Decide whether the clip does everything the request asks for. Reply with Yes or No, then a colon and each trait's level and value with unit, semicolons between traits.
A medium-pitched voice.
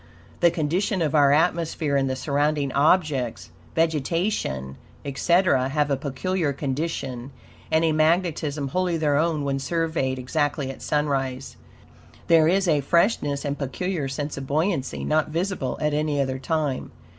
Yes: medium, 150 Hz